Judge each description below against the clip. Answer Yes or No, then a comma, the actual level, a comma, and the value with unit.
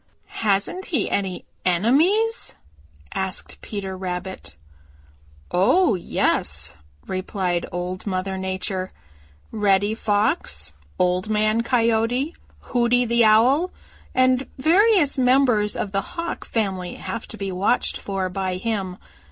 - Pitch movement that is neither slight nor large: Yes, average, 4.9 semitones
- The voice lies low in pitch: No, high, 210 Hz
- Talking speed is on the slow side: Yes, slow, 110 wpm